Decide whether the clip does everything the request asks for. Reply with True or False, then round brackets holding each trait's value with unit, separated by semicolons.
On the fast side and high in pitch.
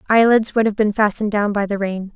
True (250 wpm; 210 Hz)